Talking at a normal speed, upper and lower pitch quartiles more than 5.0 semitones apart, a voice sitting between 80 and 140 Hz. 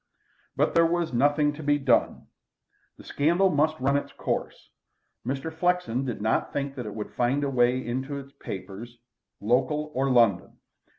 No: average, 165 wpm; average, 3.6 semitones; low, 135 Hz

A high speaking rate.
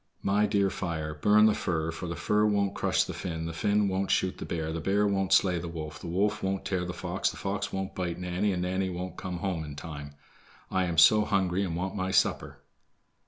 Yes: fast, 230 wpm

